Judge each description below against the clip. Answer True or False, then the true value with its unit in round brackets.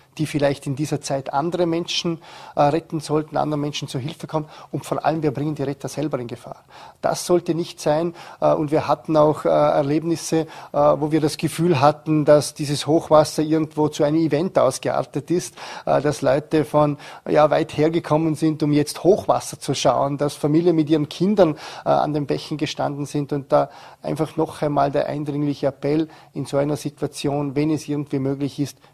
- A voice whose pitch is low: False (150 Hz)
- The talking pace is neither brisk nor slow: True (180 wpm)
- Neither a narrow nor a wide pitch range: False (1.5 semitones)